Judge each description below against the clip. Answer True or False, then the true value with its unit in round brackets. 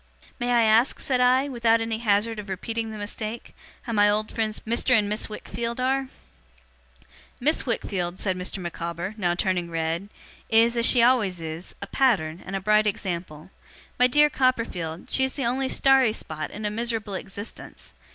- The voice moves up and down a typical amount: True (4.2 semitones)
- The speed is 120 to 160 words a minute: False (175 wpm)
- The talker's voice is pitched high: True (215 Hz)